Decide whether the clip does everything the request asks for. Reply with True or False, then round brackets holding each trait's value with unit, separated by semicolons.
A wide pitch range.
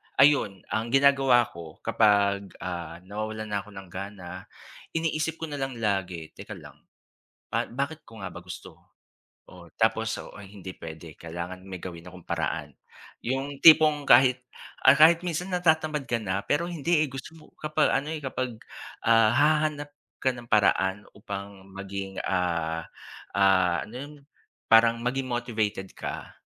True (6.7 semitones)